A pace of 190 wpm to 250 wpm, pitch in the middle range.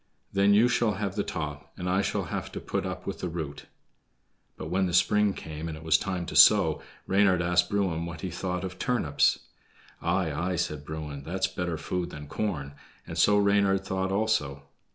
No: average, 195 wpm; very low, 90 Hz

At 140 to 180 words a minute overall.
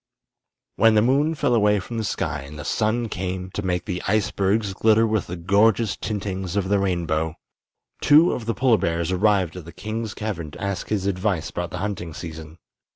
No: average, 195 wpm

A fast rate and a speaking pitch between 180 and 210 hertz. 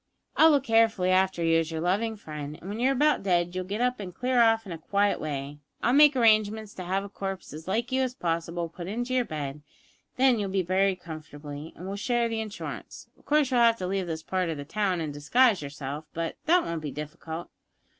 Yes: fast, 235 wpm; high, 190 Hz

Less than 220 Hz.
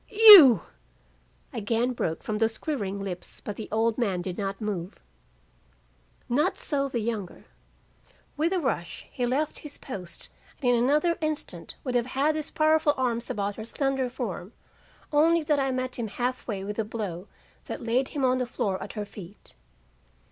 No: high, 240 Hz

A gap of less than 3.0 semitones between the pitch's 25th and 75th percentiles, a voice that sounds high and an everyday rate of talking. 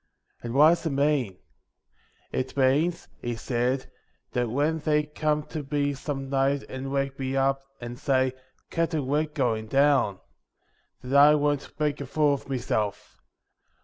No: narrow, 2.4 semitones; medium, 140 Hz; average, 165 wpm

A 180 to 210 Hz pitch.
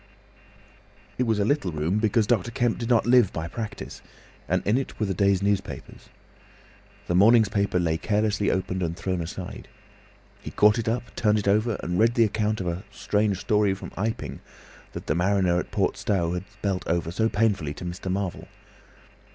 No: low, 100 Hz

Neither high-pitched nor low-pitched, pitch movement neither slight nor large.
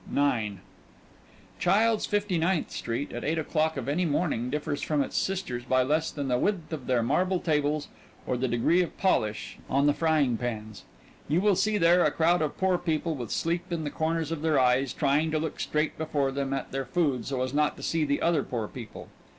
Yes: medium, 150 Hz; average, 4.1 semitones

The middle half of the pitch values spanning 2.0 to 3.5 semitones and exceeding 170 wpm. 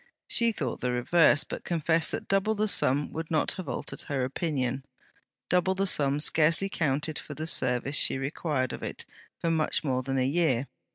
No: average, 4.2 semitones; average, 185 wpm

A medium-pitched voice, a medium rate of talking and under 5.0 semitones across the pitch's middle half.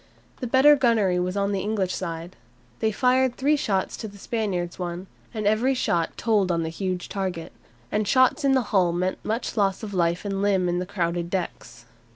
No: high, 195 Hz; average, 195 wpm; average, 3.8 semitones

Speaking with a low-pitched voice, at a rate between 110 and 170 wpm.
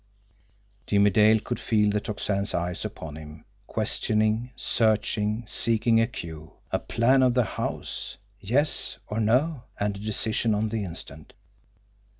Yes: low, 105 Hz; average, 140 wpm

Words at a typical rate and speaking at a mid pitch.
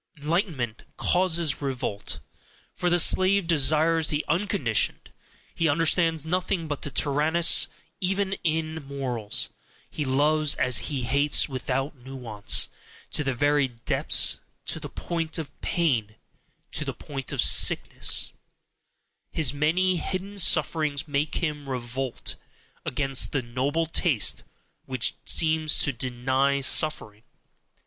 No: slow, 120 wpm; medium, 150 Hz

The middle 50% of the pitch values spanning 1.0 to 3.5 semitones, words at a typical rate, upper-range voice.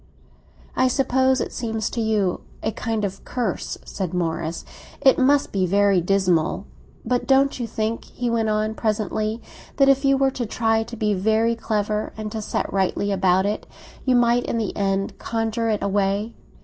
Yes: average, 3.1 semitones; average, 175 wpm; high, 220 Hz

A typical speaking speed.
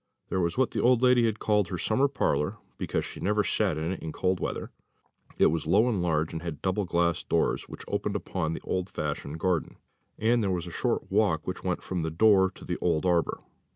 No: fast, 225 wpm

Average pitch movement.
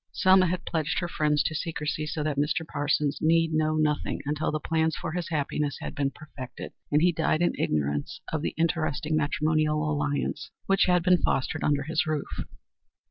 No: narrow, 1.7 semitones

